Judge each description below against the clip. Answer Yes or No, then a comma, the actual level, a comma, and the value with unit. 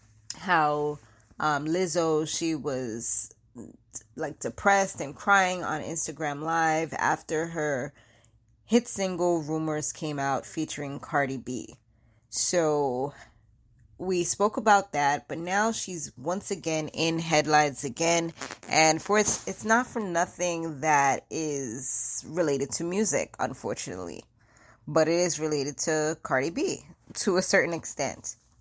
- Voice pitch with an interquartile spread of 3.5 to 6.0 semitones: Yes, average, 4.2 semitones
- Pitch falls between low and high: Yes, medium, 155 Hz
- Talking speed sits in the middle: No, slow, 125 wpm